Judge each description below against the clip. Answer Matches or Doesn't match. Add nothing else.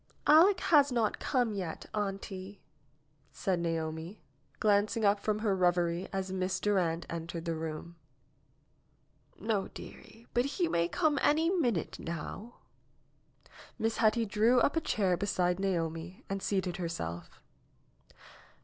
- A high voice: Matches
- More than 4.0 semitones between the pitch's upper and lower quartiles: Matches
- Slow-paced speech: Matches